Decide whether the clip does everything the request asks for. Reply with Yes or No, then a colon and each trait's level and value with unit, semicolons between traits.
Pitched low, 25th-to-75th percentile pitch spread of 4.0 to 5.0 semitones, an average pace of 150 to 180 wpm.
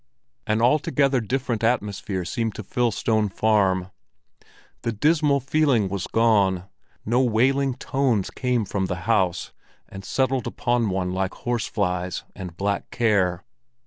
No: low, 110 Hz; average, 4.6 semitones; slow, 135 wpm